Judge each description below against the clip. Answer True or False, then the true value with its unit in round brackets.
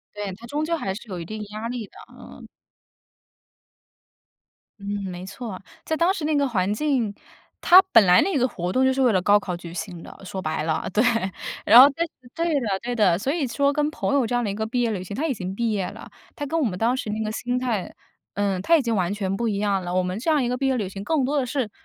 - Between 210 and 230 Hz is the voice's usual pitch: True (225 Hz)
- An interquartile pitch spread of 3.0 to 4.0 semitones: False (5.3 semitones)